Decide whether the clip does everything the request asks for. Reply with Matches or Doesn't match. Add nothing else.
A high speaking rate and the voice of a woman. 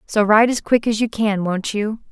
Matches